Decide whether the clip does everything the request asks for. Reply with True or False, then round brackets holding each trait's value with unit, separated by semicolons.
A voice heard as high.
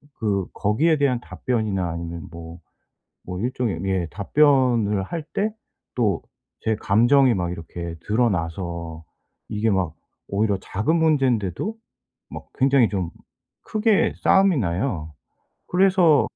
False (105 Hz)